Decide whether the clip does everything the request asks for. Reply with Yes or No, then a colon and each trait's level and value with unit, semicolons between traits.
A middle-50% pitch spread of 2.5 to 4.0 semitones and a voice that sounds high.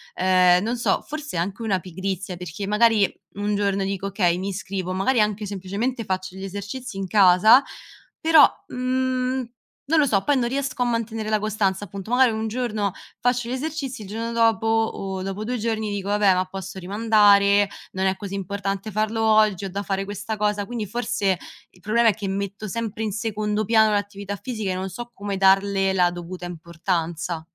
Yes: average, 2.8 semitones; high, 205 Hz